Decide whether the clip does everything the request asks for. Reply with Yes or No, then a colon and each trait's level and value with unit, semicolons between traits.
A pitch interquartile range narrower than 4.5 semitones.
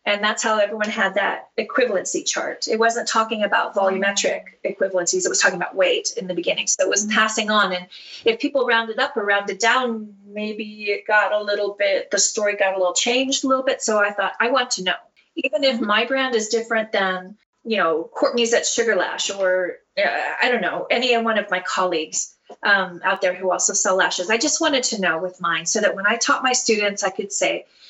Yes: average, 3.2 semitones